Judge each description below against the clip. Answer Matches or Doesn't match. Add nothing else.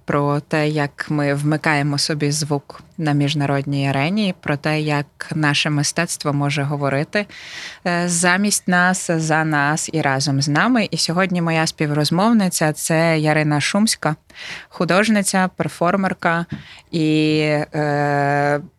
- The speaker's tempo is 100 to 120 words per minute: Matches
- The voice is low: Doesn't match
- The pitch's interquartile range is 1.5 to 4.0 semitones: Matches